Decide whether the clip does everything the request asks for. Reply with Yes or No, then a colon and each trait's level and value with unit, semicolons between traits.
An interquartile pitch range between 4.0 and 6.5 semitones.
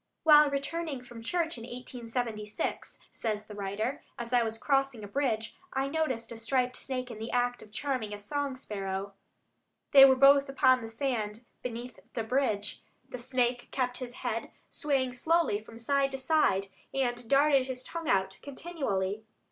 No: average, 3.6 semitones